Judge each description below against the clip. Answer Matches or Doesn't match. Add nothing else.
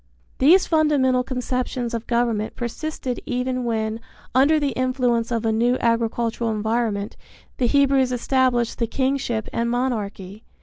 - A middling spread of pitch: Doesn't match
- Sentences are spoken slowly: Matches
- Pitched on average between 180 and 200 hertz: Doesn't match